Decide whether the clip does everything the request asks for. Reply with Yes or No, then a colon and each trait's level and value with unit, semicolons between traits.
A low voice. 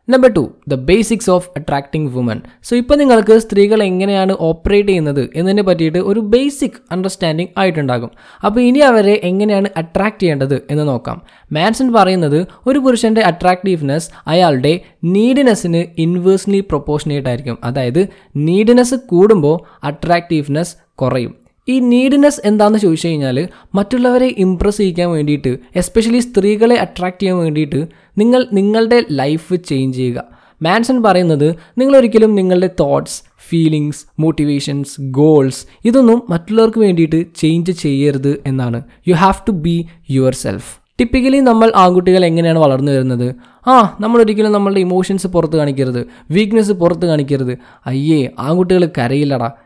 No: medium, 180 Hz